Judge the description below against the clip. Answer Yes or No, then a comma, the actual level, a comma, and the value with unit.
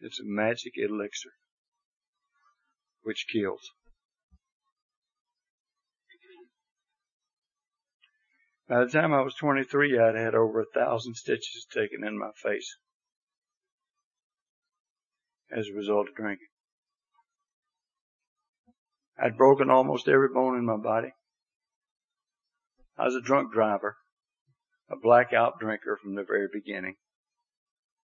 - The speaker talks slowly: Yes, slow, 100 wpm